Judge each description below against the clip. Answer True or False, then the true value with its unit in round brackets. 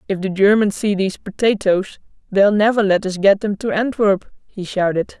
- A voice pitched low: False (200 Hz)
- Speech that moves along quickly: False (185 wpm)